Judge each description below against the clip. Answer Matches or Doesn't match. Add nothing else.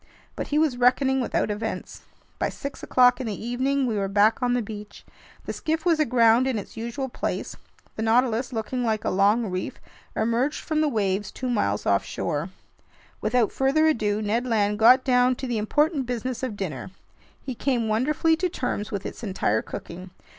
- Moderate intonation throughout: Matches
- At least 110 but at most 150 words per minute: Doesn't match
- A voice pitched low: Doesn't match